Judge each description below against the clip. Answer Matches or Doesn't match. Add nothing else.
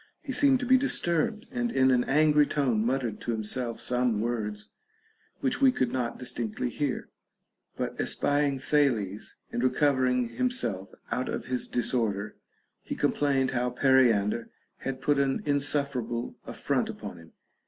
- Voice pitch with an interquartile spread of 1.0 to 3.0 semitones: Doesn't match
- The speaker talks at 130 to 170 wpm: Matches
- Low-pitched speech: Matches